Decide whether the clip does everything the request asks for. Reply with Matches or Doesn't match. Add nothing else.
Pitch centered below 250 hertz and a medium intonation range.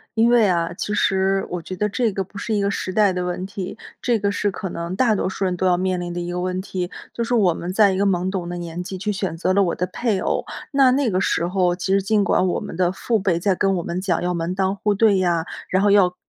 Doesn't match